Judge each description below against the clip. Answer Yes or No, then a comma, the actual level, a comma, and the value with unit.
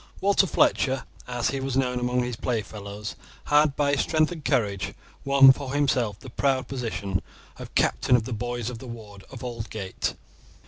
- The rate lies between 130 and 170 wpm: No, average, 180 wpm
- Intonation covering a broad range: No, average, 3.5 semitones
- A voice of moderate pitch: No, low, 125 Hz